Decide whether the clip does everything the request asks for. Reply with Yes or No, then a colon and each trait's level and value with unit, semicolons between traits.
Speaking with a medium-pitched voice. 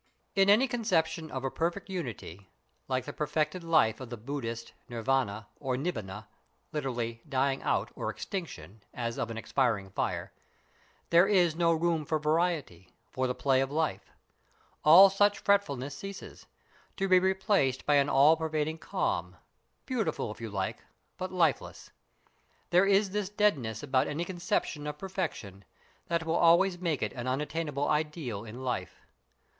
Yes: medium, 150 Hz